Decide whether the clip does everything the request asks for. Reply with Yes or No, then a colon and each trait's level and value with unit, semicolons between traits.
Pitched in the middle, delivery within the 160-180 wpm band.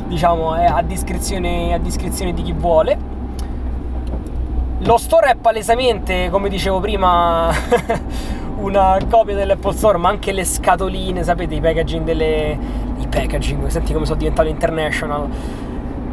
No: medium, 165 Hz; average, 130 wpm